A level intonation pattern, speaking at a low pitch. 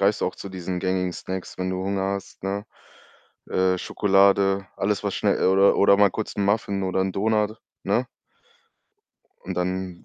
Yes: narrow, 1.2 semitones; very low, 95 Hz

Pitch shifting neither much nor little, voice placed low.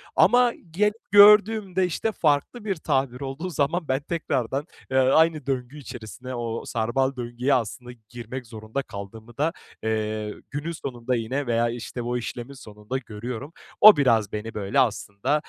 Yes: average, 4.6 semitones; low, 130 Hz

